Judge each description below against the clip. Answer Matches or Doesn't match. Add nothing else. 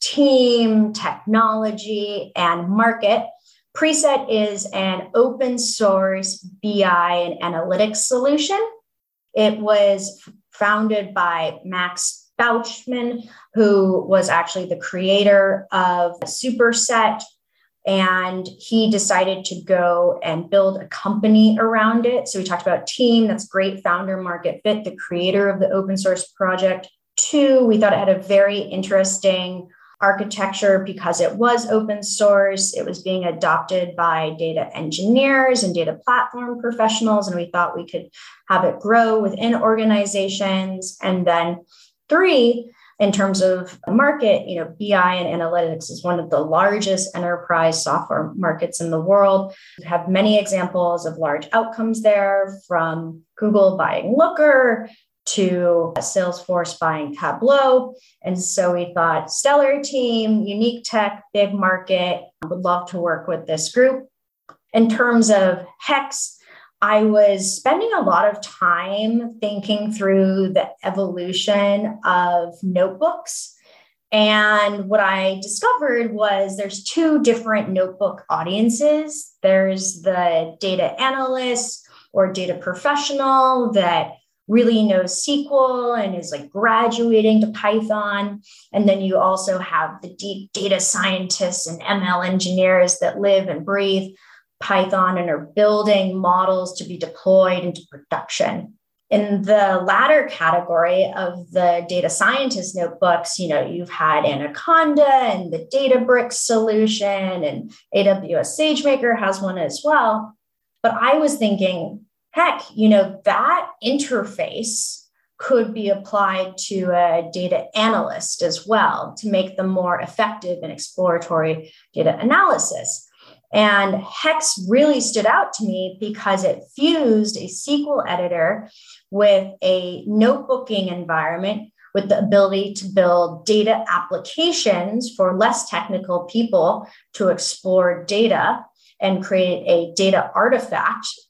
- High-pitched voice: Matches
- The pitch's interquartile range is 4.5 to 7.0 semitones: Doesn't match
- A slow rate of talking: Matches